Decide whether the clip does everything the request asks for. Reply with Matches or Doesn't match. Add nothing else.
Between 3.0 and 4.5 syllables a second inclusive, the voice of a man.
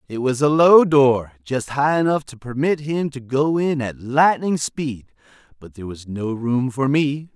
Matches